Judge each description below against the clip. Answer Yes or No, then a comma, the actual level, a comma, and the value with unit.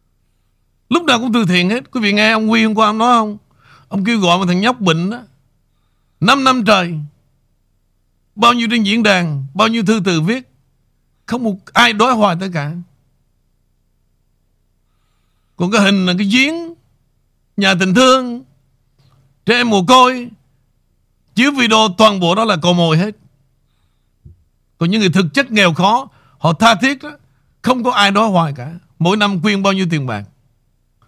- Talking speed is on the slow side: No, average, 175 wpm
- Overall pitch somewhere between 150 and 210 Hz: Yes, medium, 185 Hz